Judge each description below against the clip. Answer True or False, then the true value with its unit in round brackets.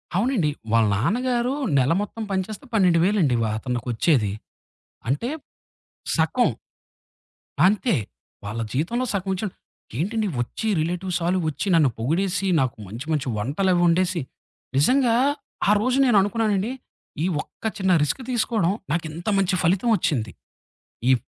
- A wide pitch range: True (6.8 semitones)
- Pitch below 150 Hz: False (180 Hz)